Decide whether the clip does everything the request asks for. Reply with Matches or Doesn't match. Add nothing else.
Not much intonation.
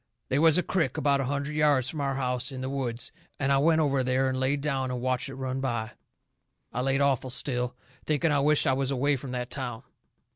Matches